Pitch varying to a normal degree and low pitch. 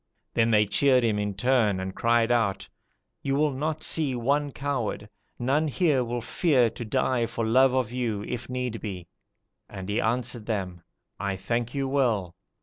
Yes: average, 3.9 semitones; low, 120 Hz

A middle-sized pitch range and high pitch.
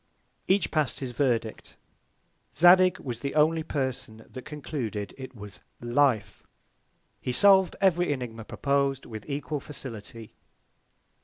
No: average, 4.7 semitones; low, 135 Hz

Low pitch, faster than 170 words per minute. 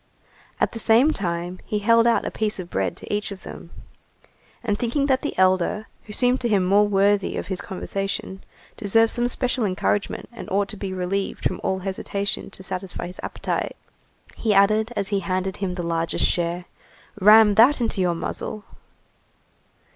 No: high, 200 Hz; average, 180 wpm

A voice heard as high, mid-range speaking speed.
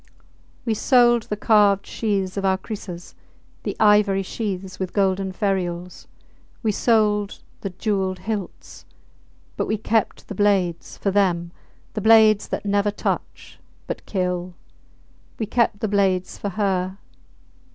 No: high, 200 Hz; slow, 130 wpm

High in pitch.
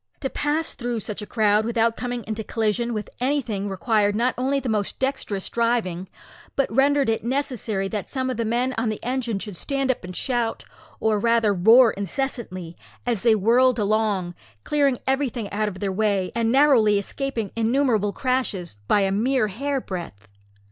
Yes: high, 225 Hz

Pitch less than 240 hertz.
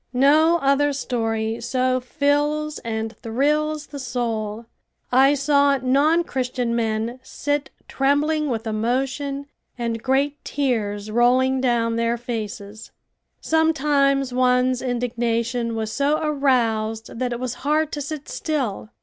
No: very high, 255 Hz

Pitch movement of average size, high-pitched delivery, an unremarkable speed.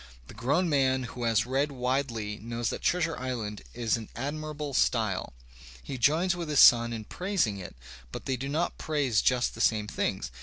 No: average, 4.4 semitones; low, 130 Hz; average, 185 wpm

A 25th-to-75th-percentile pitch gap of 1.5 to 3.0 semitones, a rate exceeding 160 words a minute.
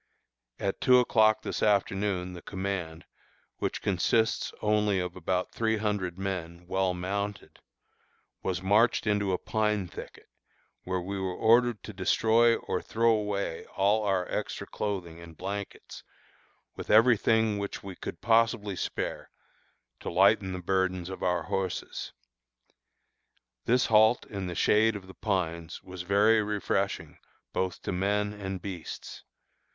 No: narrow, 2.6 semitones; average, 140 wpm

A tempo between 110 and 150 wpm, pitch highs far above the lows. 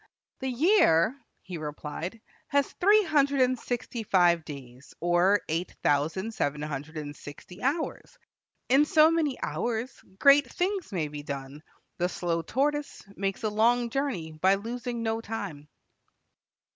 Yes: average, 140 wpm; wide, 8.7 semitones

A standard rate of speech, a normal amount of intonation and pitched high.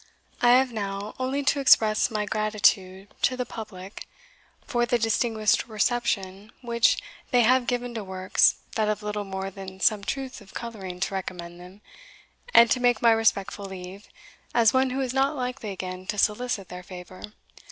Yes: average, 170 wpm; average, 4.0 semitones; high, 215 Hz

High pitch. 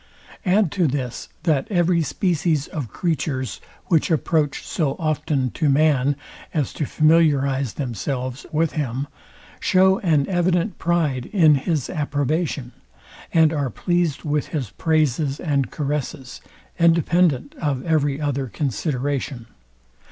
No: medium, 150 Hz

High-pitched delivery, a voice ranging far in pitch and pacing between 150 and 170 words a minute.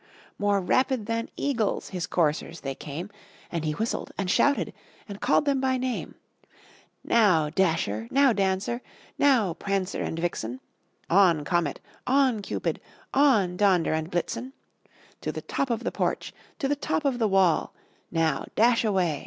Yes: high, 195 Hz; wide, 6.5 semitones; average, 155 wpm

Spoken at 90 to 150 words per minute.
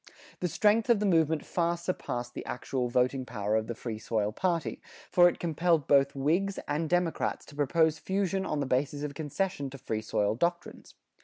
No: average, 185 wpm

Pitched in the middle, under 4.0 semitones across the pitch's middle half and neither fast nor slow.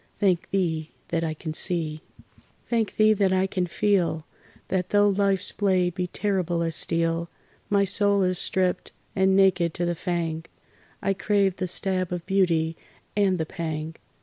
Yes: medium, 180 Hz; average, 2.8 semitones; average, 160 wpm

